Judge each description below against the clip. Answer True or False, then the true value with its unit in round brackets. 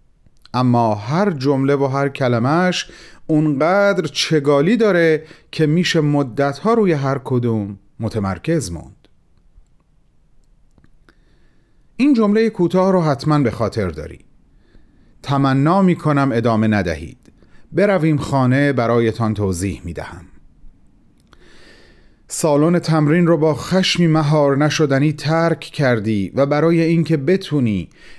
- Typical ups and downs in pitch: False (6.0 semitones)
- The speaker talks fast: False (105 wpm)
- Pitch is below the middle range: False (145 Hz)